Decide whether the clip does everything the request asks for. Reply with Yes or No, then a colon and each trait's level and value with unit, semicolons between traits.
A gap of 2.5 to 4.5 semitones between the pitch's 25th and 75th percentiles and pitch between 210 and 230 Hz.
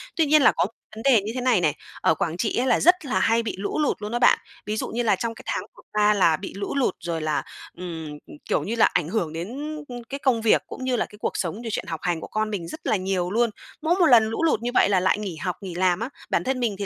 No: average, 5.2 semitones; high, 215 Hz